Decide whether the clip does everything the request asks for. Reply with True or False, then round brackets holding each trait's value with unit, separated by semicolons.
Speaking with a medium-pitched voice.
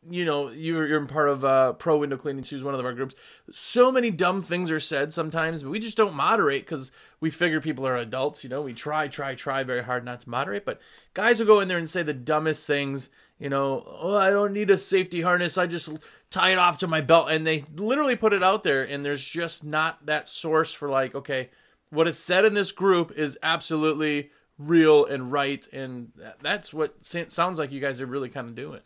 True (155 Hz)